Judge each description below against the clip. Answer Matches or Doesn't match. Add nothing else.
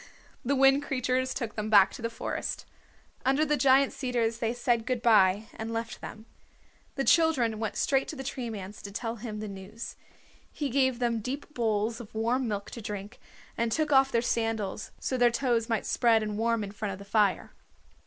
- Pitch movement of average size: Matches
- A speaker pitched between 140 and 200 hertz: Doesn't match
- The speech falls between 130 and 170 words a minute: Doesn't match